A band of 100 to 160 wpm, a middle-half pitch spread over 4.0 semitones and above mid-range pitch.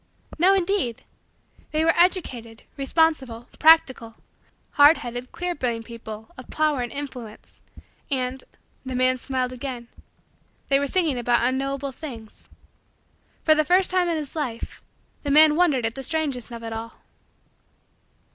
Yes: average, 140 wpm; average, 4.5 semitones; very high, 265 Hz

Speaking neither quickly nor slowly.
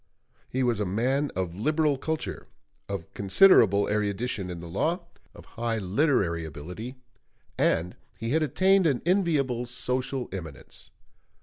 No: slow, 130 wpm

